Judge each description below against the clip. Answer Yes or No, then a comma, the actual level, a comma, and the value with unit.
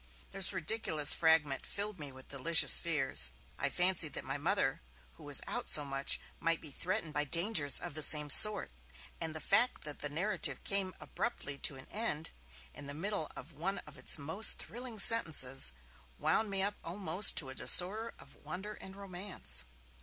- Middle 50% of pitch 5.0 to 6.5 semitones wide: Yes, average, 5.3 semitones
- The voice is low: No, medium, 165 Hz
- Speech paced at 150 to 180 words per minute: Yes, average, 175 wpm